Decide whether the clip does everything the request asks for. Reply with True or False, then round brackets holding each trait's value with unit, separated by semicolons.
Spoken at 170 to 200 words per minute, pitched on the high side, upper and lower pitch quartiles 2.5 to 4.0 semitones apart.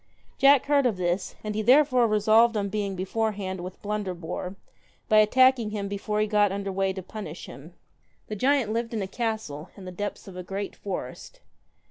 True (185 wpm; 210 Hz; 2.8 semitones)